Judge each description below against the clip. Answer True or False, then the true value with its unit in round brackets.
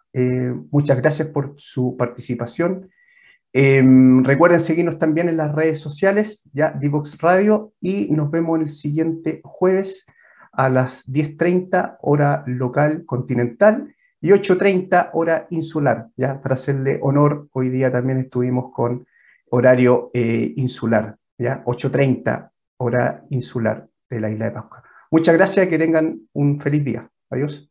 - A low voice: False (145 Hz)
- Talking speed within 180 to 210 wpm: False (135 wpm)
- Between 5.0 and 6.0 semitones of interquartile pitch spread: False (4.6 semitones)